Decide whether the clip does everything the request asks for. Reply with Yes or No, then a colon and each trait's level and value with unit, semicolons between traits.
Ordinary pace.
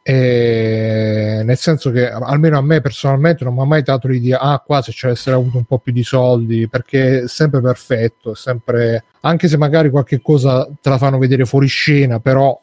No: fast, 200 wpm